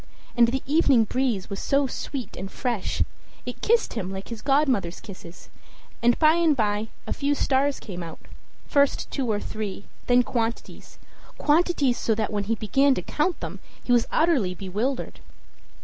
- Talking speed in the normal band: Yes, average, 170 wpm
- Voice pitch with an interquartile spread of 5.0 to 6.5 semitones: Yes, average, 5.3 semitones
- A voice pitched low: No, high, 240 Hz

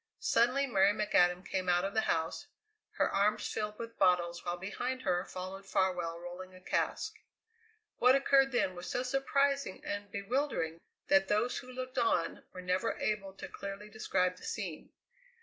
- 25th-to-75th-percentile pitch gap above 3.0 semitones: Yes, average, 5.0 semitones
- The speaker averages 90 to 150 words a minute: No, average, 165 wpm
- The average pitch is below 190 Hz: No, high, 200 Hz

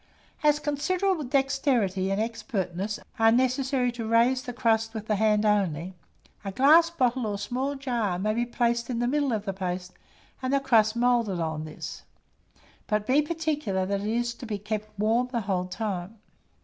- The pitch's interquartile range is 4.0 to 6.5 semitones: Yes, average, 4.3 semitones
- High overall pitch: Yes, high, 230 Hz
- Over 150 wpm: Yes, average, 170 wpm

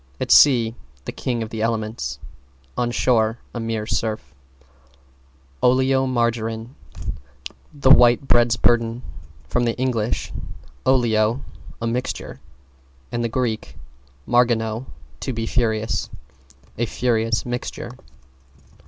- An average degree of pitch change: No, narrow, 1.7 semitones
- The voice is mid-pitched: No, low, 115 Hz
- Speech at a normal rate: No, slow, 100 wpm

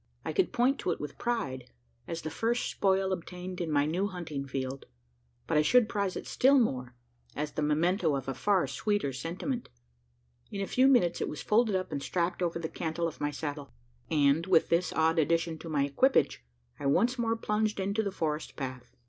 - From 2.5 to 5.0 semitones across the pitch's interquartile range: No, wide, 5.6 semitones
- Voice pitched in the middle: Yes, medium, 170 Hz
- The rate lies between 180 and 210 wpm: Yes, average, 200 wpm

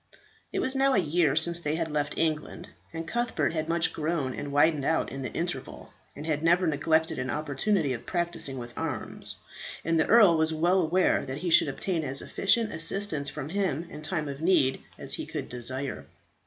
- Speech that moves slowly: No, average, 195 wpm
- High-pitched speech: No, medium, 160 Hz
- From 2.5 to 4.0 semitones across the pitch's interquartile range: Yes, average, 3.2 semitones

